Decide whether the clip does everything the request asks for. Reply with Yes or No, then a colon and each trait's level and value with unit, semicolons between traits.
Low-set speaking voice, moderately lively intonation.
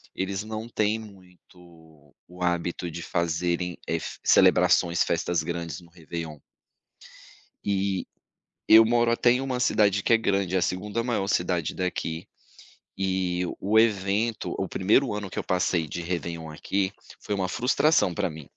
Yes: very low, 95 Hz; average, 3.4 semitones